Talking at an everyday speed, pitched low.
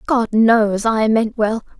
No: average, 165 wpm; high, 220 Hz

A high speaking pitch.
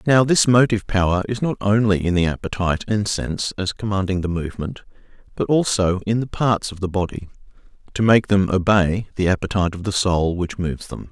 No: low, 100 Hz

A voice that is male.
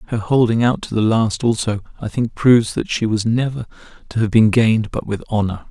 Yes: male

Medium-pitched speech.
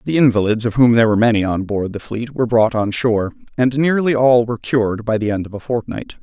No: low, 115 Hz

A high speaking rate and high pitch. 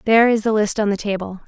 Yes: fast, 285 wpm; high, 210 Hz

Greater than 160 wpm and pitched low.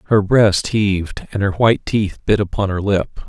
Yes: average, 200 wpm; low, 100 Hz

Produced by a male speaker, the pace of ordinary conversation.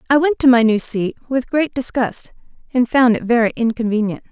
No: female; average, 195 wpm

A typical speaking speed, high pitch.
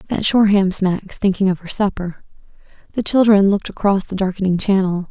Yes: average, 165 wpm; high, 195 Hz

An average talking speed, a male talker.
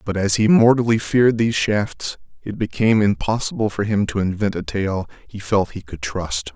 Yes: average, 190 wpm; male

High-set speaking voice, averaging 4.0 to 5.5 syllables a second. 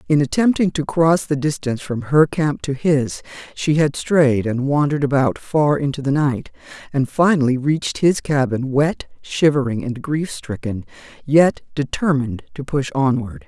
No: medium, 145 Hz; 4.6 syllables/s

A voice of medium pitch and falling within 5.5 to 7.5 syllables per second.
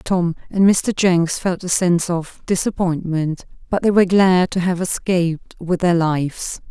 No: medium, 175 Hz; 4.4 syllables/s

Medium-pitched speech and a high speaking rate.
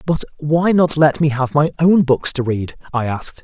Yes: medium, 145 Hz; fast, 225 wpm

